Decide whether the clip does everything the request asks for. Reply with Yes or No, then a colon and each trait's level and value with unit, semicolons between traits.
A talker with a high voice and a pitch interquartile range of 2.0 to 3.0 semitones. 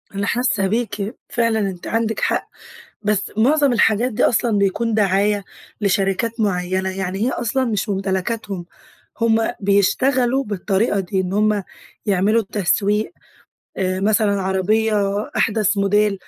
Yes: high, 205 Hz; average, 2.7 semitones